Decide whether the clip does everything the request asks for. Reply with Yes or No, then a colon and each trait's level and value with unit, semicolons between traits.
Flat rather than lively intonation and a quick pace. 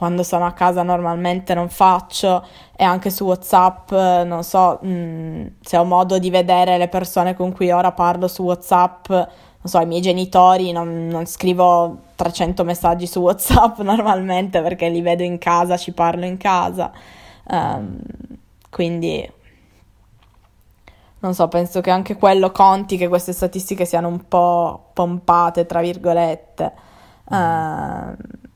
No: narrow, 1.2 semitones; average, 145 wpm